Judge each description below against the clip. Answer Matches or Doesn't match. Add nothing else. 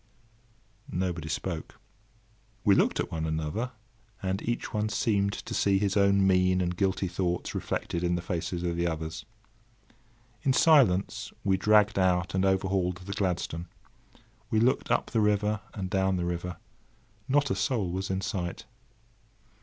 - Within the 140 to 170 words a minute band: Matches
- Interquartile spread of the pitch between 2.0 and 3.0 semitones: Matches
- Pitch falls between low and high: Doesn't match